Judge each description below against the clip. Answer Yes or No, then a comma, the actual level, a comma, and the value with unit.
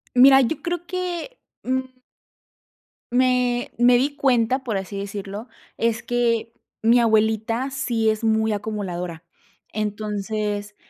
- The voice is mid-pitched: No, high, 230 Hz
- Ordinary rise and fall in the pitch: Yes, average, 3.4 semitones